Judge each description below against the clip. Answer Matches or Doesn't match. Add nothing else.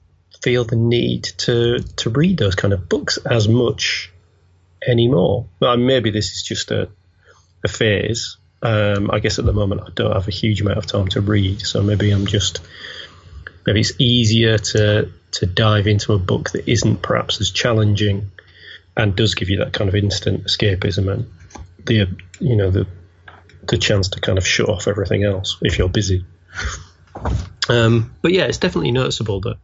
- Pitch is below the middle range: Matches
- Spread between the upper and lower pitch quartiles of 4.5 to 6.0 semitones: Doesn't match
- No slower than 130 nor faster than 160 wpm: Doesn't match